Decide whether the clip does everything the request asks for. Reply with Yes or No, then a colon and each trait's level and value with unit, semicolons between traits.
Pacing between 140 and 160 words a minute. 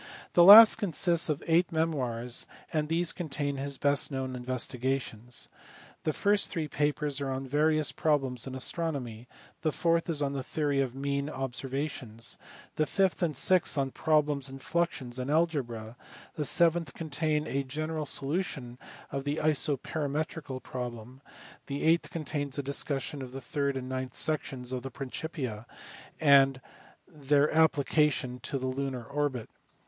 Yes: average, 150 wpm